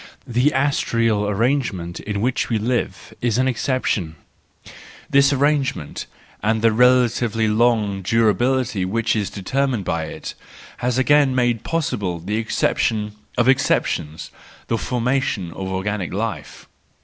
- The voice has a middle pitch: No, low, 115 Hz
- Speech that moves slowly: Yes, slow, 125 wpm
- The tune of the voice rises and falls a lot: No, average, 3.8 semitones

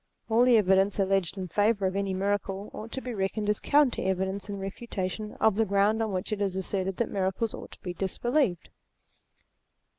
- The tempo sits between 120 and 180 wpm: No, average, 190 wpm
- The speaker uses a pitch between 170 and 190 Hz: No, high, 200 Hz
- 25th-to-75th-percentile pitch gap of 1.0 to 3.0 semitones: Yes, narrow, 2.4 semitones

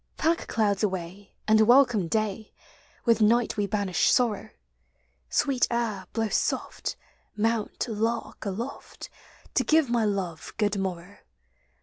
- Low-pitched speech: No, high, 215 Hz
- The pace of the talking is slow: Yes, slow, 120 wpm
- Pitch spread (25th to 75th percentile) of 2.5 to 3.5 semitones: Yes, average, 2.9 semitones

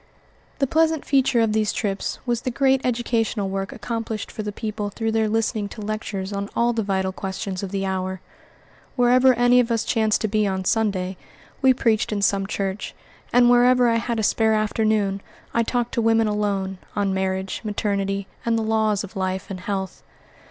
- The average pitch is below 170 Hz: No, high, 215 Hz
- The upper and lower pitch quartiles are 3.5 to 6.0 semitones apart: No, average, 2.9 semitones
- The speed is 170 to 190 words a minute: Yes, average, 185 wpm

